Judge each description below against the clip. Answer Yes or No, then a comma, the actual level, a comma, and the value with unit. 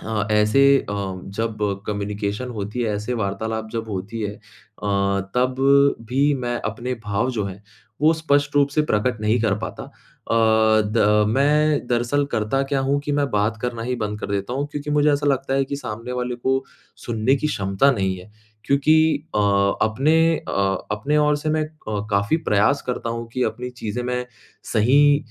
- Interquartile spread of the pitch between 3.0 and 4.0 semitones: No, average, 4.8 semitones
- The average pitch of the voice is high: No, low, 120 Hz